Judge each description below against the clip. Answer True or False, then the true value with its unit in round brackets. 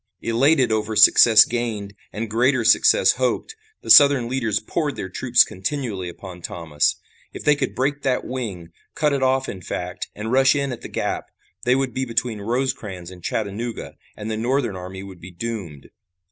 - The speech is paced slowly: False (175 wpm)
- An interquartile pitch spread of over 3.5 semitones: True (5.1 semitones)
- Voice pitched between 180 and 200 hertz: False (115 Hz)